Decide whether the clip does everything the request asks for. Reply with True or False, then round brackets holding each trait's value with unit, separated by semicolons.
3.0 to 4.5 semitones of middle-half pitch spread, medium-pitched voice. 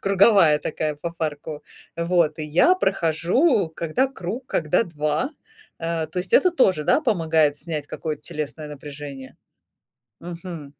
True (3.7 semitones; 165 Hz)